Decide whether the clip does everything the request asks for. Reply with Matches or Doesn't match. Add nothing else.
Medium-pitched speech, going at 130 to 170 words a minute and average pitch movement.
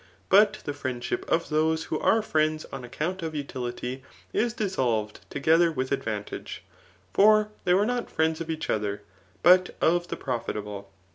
Doesn't match